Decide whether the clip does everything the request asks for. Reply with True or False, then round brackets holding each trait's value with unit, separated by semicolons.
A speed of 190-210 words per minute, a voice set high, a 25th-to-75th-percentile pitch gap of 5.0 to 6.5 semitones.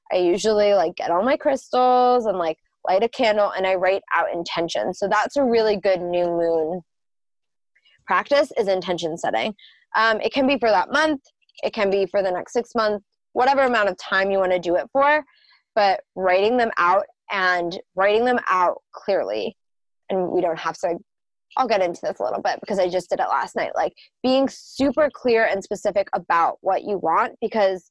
True (200 wpm; 205 Hz; 5.3 semitones)